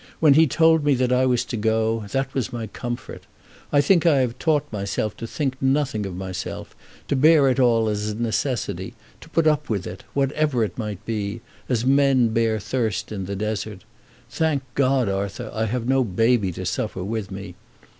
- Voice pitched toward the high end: No, low, 120 Hz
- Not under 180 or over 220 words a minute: Yes, average, 195 wpm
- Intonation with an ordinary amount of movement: Yes, average, 4.2 semitones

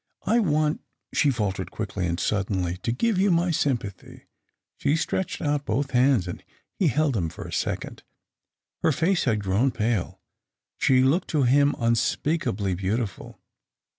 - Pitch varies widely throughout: Yes, wide, 7.2 semitones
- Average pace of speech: Yes, average, 165 wpm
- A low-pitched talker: Yes, low, 125 Hz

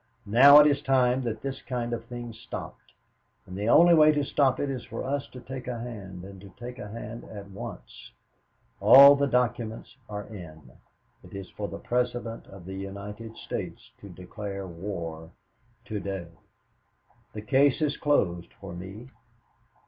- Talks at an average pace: Yes, average, 170 wpm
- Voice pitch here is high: No, low, 115 Hz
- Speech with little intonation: No, average, 4.8 semitones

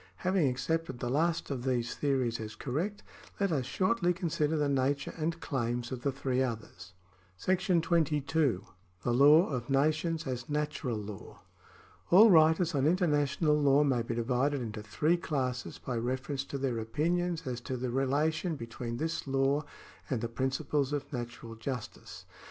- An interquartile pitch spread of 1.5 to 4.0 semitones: No, average, 4.4 semitones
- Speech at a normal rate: Yes, average, 155 wpm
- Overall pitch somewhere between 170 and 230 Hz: No, medium, 140 Hz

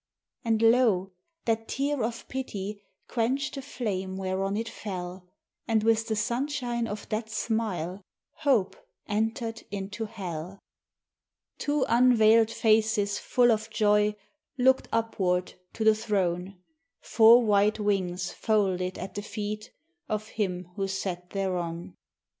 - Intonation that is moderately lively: Yes, average, 3.0 semitones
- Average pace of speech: No, slow, 125 wpm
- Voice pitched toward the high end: Yes, high, 215 Hz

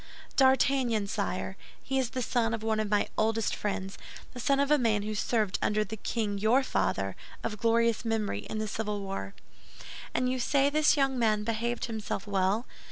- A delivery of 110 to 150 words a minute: No, average, 180 wpm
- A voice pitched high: Yes, high, 220 Hz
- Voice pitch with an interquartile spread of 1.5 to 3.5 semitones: Yes, average, 3.0 semitones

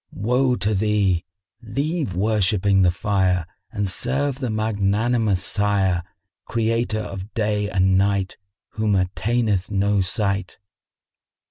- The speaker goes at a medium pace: No, slow, 110 wpm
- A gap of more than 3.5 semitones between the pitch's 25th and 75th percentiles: No, average, 2.7 semitones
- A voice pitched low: Yes, low, 105 Hz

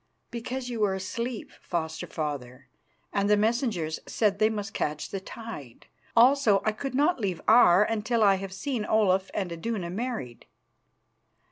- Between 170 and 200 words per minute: No, average, 150 wpm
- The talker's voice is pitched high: Yes, high, 210 Hz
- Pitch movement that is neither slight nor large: Yes, average, 4.2 semitones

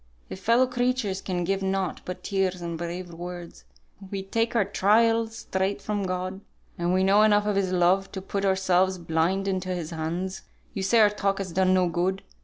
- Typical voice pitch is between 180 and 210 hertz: Yes, high, 190 Hz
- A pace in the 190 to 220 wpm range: Yes, average, 195 wpm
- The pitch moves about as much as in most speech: No, narrow, 1.9 semitones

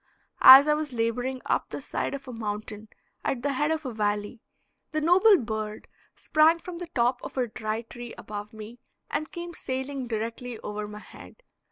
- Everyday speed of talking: Yes, average, 185 wpm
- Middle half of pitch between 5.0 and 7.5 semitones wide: Yes, wide, 5.4 semitones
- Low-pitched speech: No, high, 245 Hz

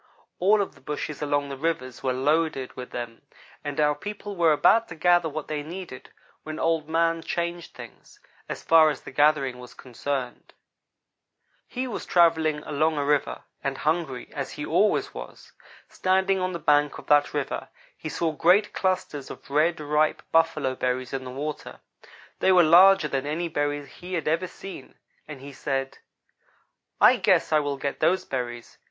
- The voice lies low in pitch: No, medium, 150 Hz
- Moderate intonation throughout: Yes, average, 3.5 semitones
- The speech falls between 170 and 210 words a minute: Yes, average, 175 wpm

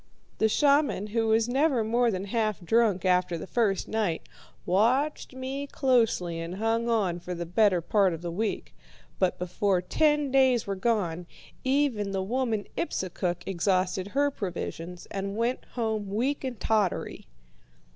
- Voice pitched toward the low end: No, high, 215 Hz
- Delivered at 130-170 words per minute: Yes, average, 150 wpm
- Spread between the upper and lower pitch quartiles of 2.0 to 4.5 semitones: No, average, 4.9 semitones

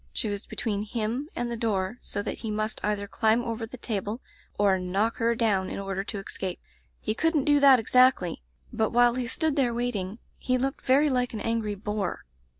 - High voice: Yes, high, 225 Hz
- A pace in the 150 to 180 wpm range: No, fast, 205 wpm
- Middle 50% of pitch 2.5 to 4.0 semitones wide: Yes, average, 3.3 semitones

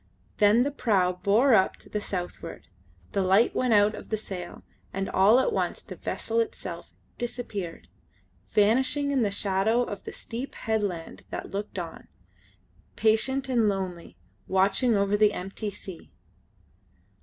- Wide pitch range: No, average, 3.8 semitones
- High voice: Yes, high, 205 Hz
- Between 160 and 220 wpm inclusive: No, average, 145 wpm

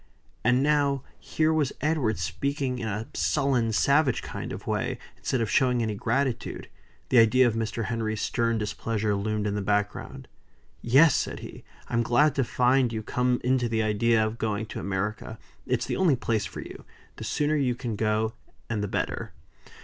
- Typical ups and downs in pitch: Yes, average, 3.3 semitones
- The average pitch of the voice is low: Yes, low, 115 Hz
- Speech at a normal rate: Yes, average, 180 wpm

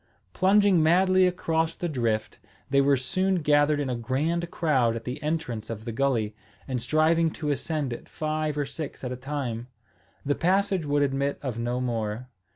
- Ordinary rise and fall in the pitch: Yes, average, 4.5 semitones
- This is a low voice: No, medium, 145 Hz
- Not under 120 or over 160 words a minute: No, average, 175 wpm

